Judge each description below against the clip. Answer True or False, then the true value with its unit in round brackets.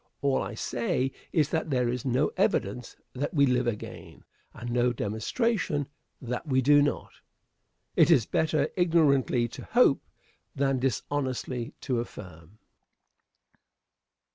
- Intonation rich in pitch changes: False (3.3 semitones)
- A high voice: False (130 Hz)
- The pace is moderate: False (125 wpm)